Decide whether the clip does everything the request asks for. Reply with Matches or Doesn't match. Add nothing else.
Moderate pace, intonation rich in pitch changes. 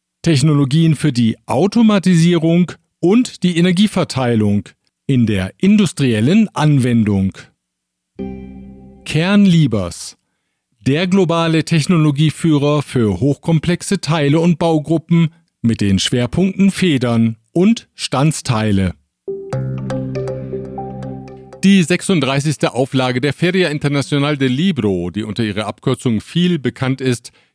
Doesn't match